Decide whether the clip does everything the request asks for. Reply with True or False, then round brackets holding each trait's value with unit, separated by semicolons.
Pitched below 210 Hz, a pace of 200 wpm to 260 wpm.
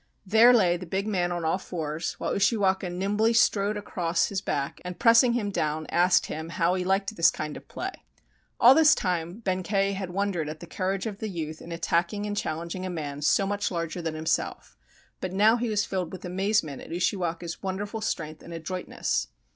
True (185 Hz; 205 wpm)